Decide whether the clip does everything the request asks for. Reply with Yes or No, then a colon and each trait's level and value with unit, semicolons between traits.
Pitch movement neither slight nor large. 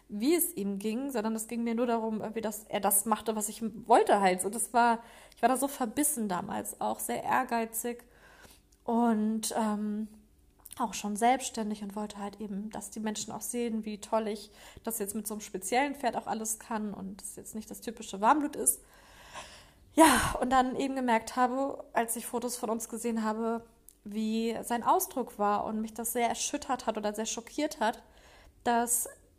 No: narrow, 1.9 semitones